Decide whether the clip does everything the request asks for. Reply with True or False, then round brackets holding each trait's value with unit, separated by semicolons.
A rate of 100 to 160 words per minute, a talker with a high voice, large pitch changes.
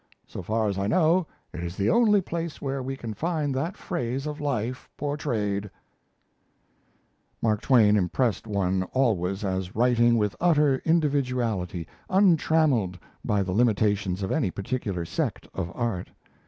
False (140 wpm; 115 Hz; 6.5 semitones)